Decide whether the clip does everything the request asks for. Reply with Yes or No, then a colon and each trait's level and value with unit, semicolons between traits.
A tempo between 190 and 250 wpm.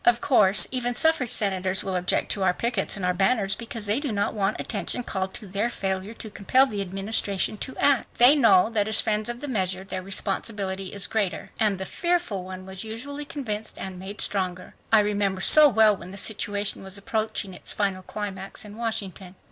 Yes: average, 200 wpm